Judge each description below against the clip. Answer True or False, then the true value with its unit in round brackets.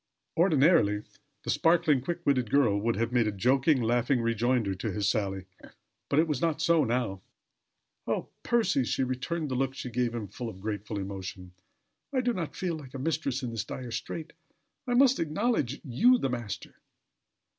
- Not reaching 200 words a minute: True (175 wpm)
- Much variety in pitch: True (6.1 semitones)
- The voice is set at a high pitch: False (125 Hz)